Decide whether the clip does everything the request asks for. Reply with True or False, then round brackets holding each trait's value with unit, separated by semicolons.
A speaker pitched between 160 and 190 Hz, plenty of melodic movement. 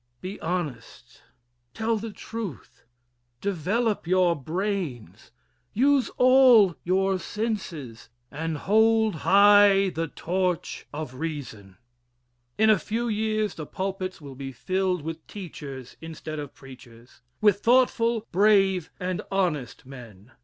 True (185 Hz; 6.2 semitones)